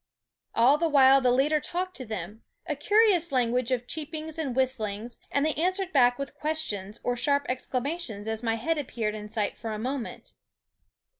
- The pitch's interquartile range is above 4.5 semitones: Yes, average, 5.2 semitones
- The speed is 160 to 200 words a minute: Yes, average, 180 wpm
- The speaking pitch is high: Yes, very high, 260 Hz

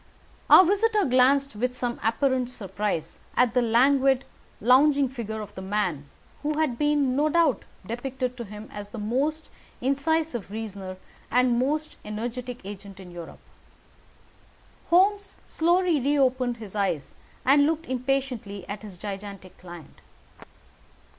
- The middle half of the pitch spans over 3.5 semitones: Yes, average, 5.3 semitones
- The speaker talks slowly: Yes, slow, 130 wpm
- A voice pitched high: Yes, very high, 250 Hz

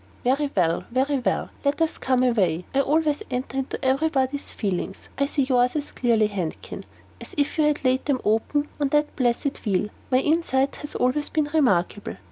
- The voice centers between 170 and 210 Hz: No, very high, 265 Hz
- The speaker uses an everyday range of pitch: Yes, average, 3.6 semitones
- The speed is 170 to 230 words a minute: Yes, average, 185 wpm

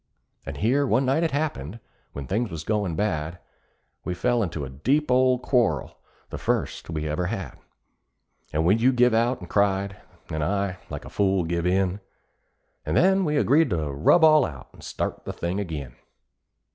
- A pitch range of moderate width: No, wide, 7.6 semitones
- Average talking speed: Yes, average, 180 wpm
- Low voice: Yes, low, 100 Hz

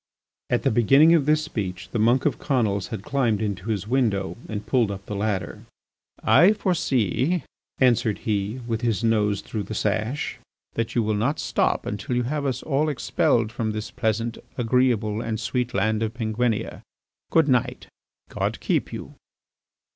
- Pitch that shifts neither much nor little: Yes, average, 3.4 semitones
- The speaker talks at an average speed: Yes, average, 165 wpm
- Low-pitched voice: Yes, low, 115 Hz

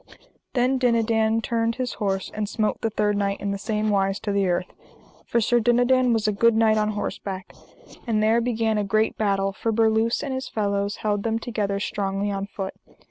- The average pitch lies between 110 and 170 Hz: No, high, 215 Hz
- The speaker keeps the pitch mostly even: Yes, narrow, 2.3 semitones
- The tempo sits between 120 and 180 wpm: No, average, 195 wpm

